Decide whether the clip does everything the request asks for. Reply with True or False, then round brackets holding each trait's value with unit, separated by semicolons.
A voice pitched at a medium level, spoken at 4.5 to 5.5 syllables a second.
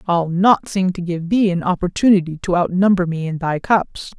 True (180 Hz; 5.0 syllables/s)